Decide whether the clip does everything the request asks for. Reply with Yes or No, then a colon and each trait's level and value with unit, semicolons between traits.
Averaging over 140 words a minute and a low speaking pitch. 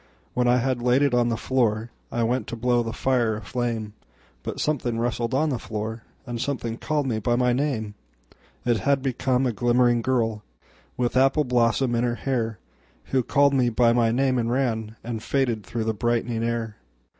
Yes: average, 170 wpm; low, 120 Hz